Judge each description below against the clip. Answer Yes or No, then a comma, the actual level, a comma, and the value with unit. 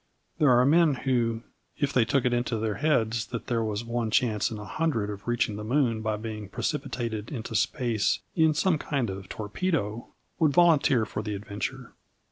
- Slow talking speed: No, average, 185 wpm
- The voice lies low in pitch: Yes, low, 115 Hz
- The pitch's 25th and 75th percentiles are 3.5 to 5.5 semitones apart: Yes, average, 4.1 semitones